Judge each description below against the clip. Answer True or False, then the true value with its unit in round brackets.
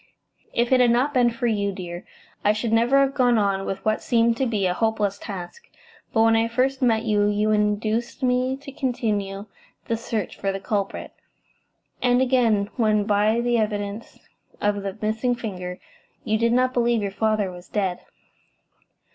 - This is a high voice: True (220 Hz)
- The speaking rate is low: False (175 wpm)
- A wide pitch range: False (2.9 semitones)